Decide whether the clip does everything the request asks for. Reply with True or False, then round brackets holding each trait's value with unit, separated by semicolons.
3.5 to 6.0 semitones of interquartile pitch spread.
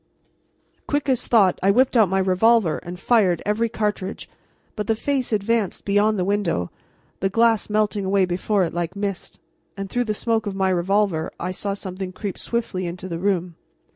False (3.1 semitones)